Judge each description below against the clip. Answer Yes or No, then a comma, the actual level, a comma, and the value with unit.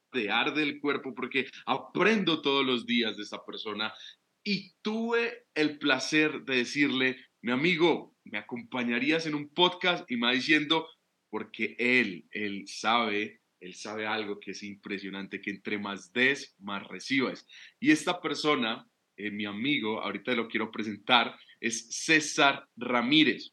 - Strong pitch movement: Yes, wide, 6.2 semitones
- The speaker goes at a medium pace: Yes, average, 150 wpm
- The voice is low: Yes, low, 125 Hz